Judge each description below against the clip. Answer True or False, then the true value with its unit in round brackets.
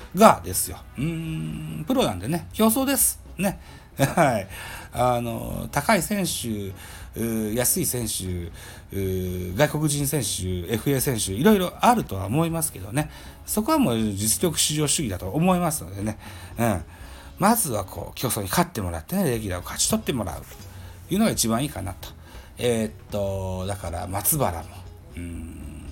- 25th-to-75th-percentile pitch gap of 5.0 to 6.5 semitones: False (8.8 semitones)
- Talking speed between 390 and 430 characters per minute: False (305 characters per minute)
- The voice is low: True (105 Hz)